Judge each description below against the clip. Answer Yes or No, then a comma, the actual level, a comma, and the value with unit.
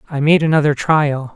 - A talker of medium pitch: Yes, medium, 150 Hz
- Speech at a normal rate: Yes, average, 175 wpm